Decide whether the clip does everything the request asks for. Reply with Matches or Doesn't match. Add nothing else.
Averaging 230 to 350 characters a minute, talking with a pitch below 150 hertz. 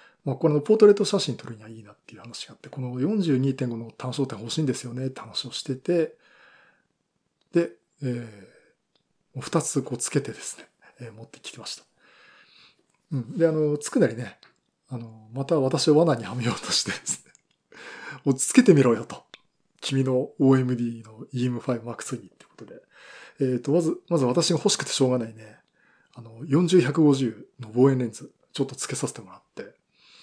Matches